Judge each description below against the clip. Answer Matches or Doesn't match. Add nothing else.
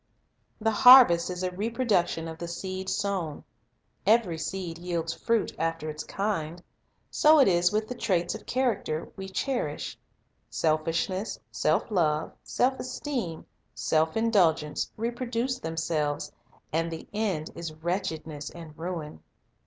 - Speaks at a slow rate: Matches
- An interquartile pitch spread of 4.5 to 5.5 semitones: Matches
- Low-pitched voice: Doesn't match